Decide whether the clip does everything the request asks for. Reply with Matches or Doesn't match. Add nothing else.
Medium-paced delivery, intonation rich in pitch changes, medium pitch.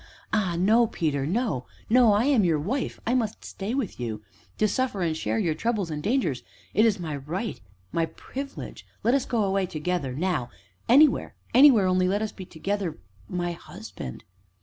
Doesn't match